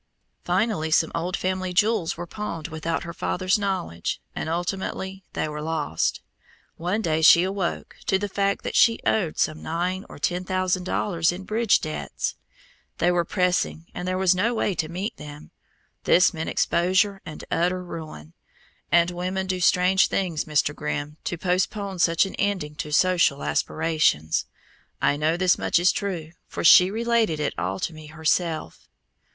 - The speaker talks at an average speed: Yes, average, 165 wpm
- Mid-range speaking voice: Yes, medium, 175 Hz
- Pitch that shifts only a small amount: No, average, 3.0 semitones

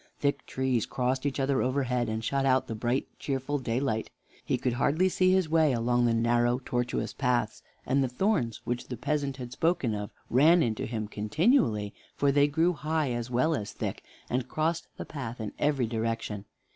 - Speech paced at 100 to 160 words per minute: No, average, 185 wpm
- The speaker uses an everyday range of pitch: Yes, average, 3.6 semitones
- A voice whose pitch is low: Yes, low, 130 Hz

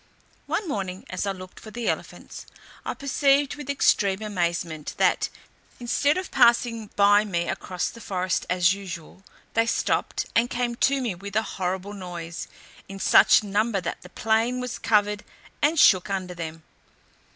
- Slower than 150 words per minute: No, average, 160 wpm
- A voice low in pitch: No, high, 205 Hz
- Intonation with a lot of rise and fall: No, average, 4.5 semitones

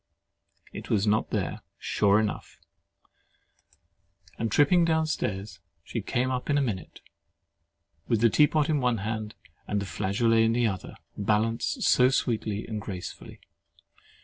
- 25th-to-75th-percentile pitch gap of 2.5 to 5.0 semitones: Yes, average, 3.5 semitones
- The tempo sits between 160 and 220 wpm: No, average, 145 wpm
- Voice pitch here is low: Yes, low, 115 Hz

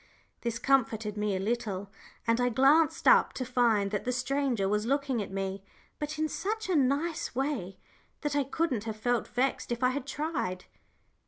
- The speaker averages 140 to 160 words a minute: No, average, 180 wpm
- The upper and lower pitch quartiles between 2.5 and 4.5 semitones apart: No, average, 4.9 semitones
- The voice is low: No, high, 245 Hz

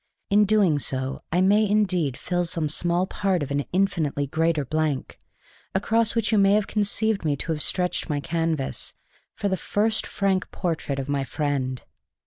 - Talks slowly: No, average, 165 wpm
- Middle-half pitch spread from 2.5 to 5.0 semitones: No, wide, 5.5 semitones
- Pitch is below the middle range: No, medium, 170 Hz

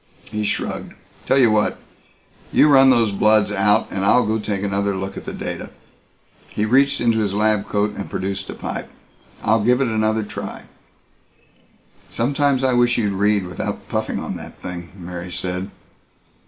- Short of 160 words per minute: No, average, 170 wpm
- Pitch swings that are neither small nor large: Yes, average, 3.1 semitones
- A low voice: Yes, low, 105 Hz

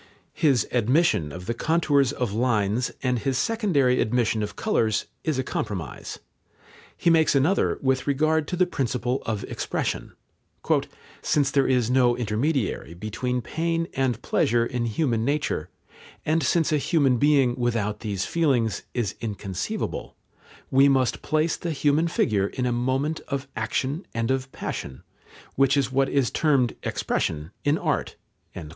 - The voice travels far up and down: No, average, 4.2 semitones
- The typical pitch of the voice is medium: No, low, 130 Hz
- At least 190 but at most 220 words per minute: No, average, 145 wpm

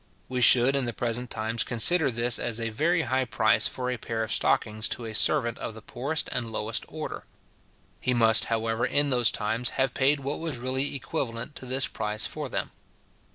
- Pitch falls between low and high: No, low, 120 Hz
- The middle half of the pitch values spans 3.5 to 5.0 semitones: No, average, 2.9 semitones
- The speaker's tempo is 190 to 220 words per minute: Yes, average, 200 wpm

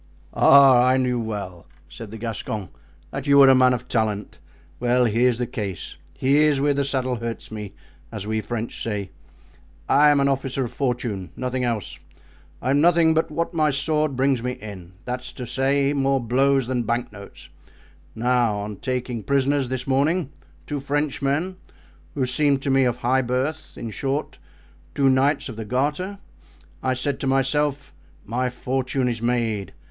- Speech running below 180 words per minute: Yes, average, 165 wpm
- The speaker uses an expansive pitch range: No, average, 3.2 semitones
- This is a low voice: Yes, low, 130 Hz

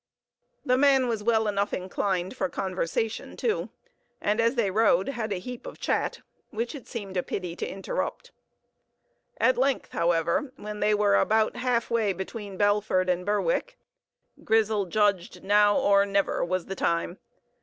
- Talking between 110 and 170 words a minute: Yes, average, 155 wpm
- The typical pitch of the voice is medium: No, high, 205 Hz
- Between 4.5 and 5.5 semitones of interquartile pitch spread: No, average, 3.4 semitones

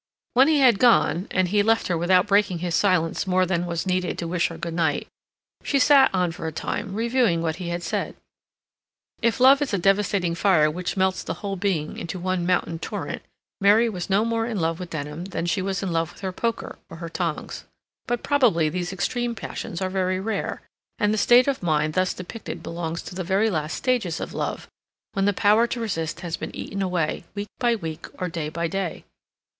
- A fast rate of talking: Yes, fast, 215 wpm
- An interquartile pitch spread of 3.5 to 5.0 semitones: Yes, average, 3.8 semitones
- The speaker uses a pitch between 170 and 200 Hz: Yes, medium, 185 Hz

